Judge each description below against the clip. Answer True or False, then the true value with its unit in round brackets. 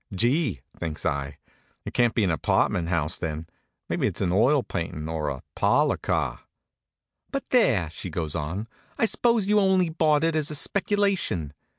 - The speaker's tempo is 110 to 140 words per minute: False (170 wpm)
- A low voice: True (105 Hz)